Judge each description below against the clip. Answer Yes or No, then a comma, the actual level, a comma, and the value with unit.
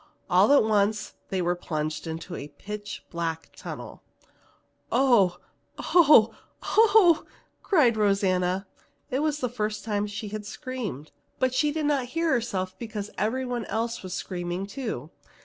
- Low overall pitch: No, high, 215 Hz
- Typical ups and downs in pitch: No, wide, 5.7 semitones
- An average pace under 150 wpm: Yes, average, 140 wpm